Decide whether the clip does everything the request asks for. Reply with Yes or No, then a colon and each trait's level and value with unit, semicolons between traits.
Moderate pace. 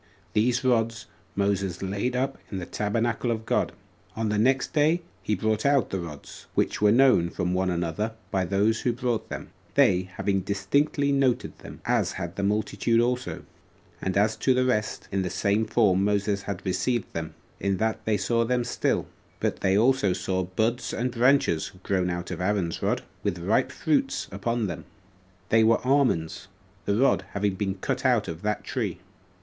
Yes: average, 180 wpm